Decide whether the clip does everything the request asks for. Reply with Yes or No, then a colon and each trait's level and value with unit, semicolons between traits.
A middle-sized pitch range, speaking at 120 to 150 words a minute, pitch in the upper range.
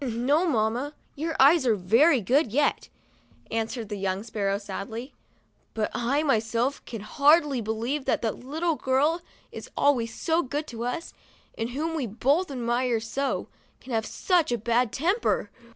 No: average, 4.7 semitones; average, 170 wpm; very high, 250 Hz